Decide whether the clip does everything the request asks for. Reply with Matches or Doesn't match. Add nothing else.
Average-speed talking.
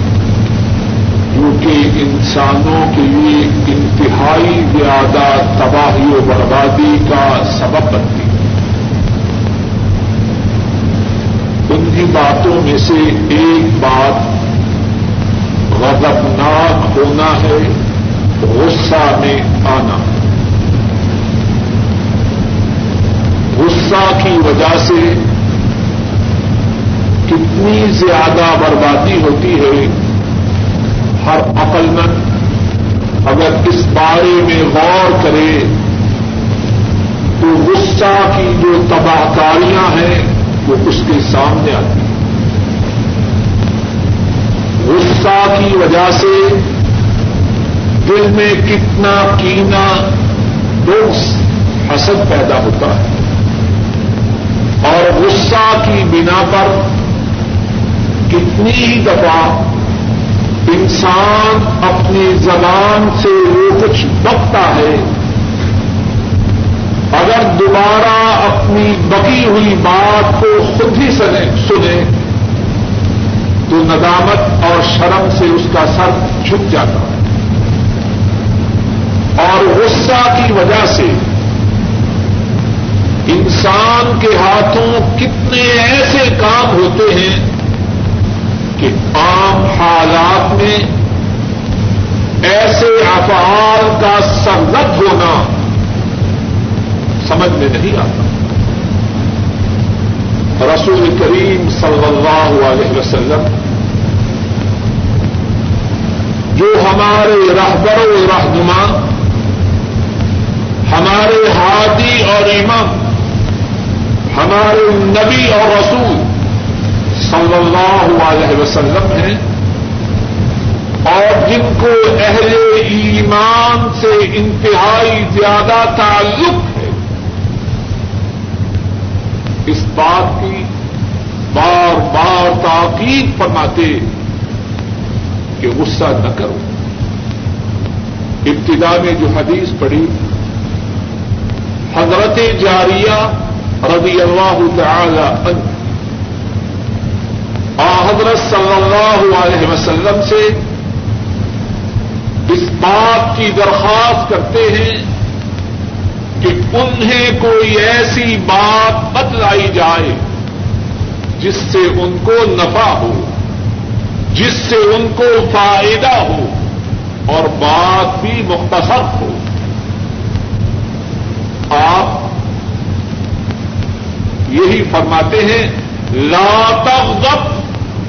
Doesn't match